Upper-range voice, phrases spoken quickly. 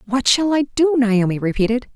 No: high, 245 Hz; average, 185 wpm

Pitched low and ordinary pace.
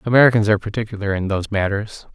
Yes: low, 105 Hz; average, 170 wpm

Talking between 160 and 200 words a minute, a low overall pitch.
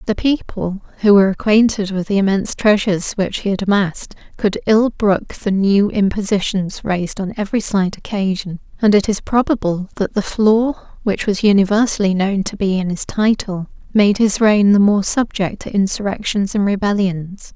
No: average, 170 wpm; high, 200 Hz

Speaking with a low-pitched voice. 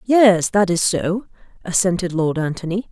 No: medium, 185 Hz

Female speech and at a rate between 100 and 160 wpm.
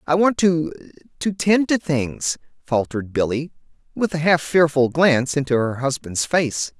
No: male; average, 150 wpm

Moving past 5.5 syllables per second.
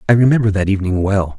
Yes: 7.3 syllables/s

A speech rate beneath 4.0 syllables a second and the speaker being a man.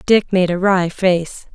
No: 3.6 syllables/s; female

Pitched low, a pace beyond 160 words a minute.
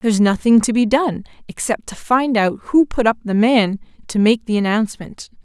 No: high, 225 Hz; average, 200 wpm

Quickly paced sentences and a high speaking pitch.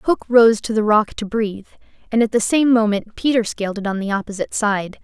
Yes: fast, 225 wpm; high, 215 Hz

